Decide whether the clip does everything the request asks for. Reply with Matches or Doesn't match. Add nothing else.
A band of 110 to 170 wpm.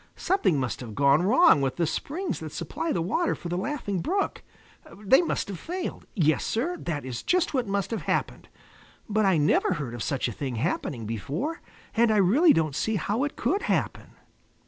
Doesn't match